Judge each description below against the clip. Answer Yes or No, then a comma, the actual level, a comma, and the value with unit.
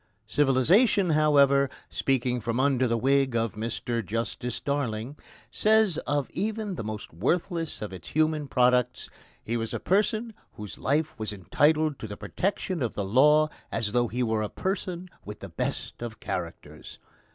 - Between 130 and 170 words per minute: Yes, average, 160 wpm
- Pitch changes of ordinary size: No, wide, 5.7 semitones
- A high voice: No, low, 130 Hz